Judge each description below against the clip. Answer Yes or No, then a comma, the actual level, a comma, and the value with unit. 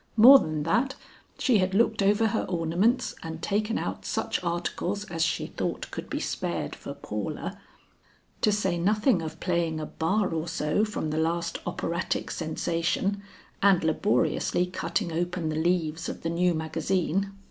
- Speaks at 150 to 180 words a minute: Yes, average, 160 wpm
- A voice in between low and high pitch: Yes, medium, 175 Hz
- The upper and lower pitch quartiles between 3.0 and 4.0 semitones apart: Yes, average, 3.6 semitones